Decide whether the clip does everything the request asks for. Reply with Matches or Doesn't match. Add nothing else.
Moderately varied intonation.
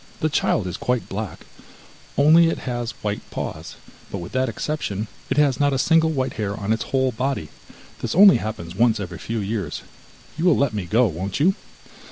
Doesn't match